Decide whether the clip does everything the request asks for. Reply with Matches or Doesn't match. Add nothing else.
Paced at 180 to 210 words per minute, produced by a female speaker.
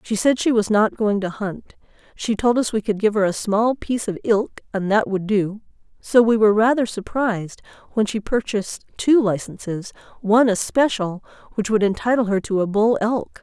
Matches